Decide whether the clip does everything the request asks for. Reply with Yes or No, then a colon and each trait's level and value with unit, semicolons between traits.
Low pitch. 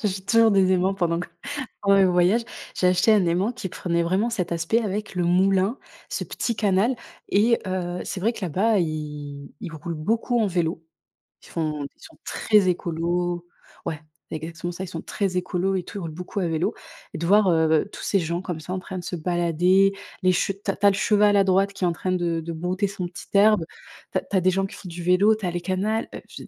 No: medium, 185 Hz